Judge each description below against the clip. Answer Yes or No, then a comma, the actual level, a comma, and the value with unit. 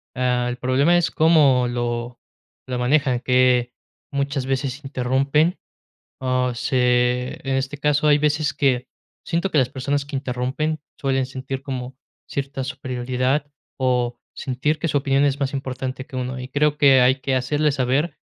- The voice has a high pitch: No, low, 130 Hz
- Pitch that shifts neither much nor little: No, narrow, 2.2 semitones